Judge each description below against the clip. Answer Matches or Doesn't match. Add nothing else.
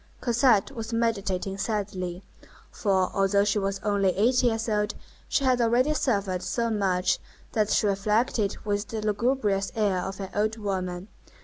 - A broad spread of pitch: Doesn't match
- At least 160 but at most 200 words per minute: Doesn't match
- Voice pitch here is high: Matches